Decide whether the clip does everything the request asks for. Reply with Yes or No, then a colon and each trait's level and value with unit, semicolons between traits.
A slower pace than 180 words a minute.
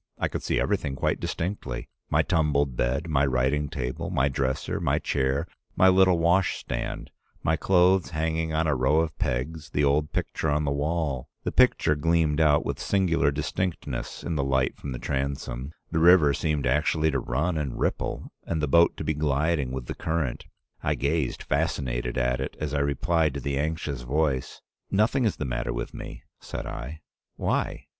No: average, 185 wpm